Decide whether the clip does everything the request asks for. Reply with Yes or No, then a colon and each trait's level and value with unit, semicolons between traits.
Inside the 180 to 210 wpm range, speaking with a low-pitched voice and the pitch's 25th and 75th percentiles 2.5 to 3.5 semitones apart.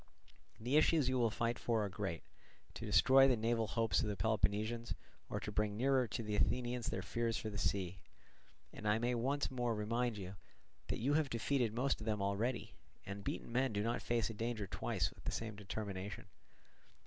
Yes: average, 195 wpm; low, 115 Hz; average, 2.9 semitones